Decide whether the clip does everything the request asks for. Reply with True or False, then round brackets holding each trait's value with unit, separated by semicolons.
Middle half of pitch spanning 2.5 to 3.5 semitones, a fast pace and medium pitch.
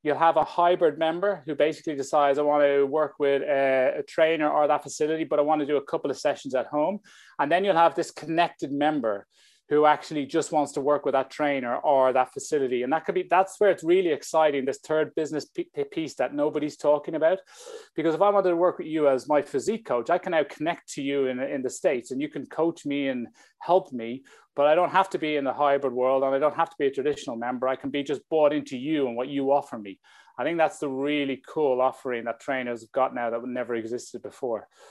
True (3.2 semitones; 245 wpm; 150 Hz)